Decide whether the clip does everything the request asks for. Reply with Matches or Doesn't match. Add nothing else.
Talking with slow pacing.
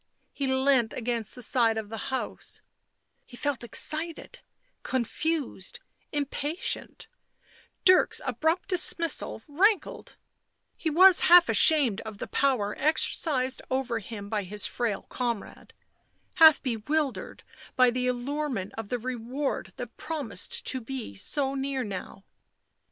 Matches